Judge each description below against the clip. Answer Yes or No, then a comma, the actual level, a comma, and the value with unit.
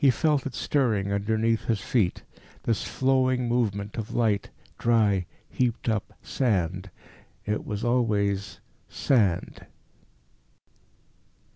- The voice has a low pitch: Yes, low, 110 Hz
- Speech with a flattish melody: No, average, 3.4 semitones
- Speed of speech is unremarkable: No, slow, 105 wpm